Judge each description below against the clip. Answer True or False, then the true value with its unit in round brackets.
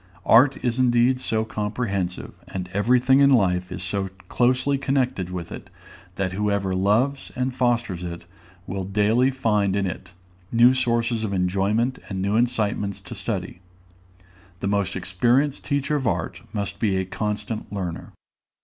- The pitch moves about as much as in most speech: True (4.4 semitones)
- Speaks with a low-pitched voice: True (105 Hz)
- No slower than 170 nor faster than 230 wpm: False (150 wpm)